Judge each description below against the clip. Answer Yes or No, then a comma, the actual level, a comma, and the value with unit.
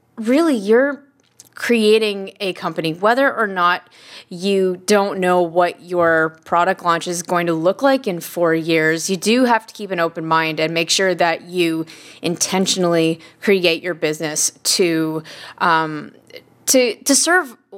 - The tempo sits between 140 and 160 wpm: Yes, average, 150 wpm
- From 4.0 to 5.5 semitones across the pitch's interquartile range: Yes, average, 4.3 semitones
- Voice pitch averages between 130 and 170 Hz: No, medium, 180 Hz